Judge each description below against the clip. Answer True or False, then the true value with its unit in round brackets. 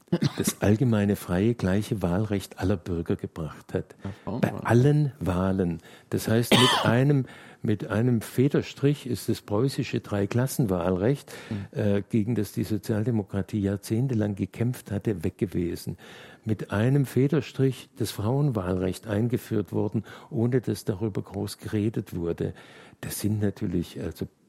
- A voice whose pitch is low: True (110 Hz)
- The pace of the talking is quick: False (125 wpm)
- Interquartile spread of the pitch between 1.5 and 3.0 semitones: False (3.6 semitones)